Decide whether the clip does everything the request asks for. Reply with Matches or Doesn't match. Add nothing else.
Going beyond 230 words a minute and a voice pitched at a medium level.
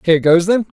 Doesn't match